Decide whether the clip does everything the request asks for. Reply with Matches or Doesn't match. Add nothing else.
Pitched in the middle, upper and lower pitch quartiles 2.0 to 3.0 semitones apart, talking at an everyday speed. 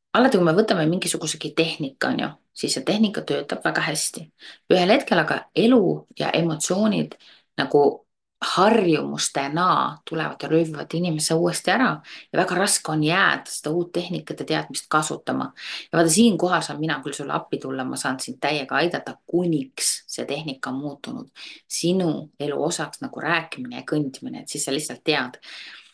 Matches